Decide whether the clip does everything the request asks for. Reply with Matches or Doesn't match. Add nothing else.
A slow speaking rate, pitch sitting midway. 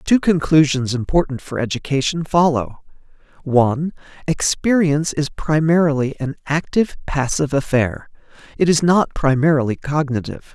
Matches